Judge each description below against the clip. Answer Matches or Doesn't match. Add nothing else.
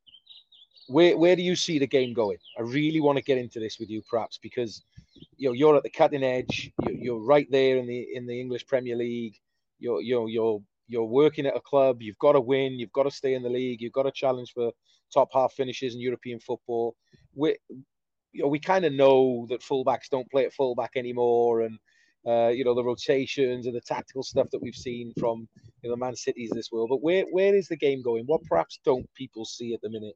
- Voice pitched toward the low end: Matches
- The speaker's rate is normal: Doesn't match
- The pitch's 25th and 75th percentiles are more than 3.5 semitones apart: Doesn't match